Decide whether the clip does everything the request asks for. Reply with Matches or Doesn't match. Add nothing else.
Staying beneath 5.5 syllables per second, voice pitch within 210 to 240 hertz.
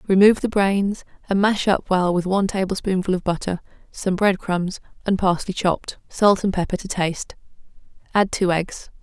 Doesn't match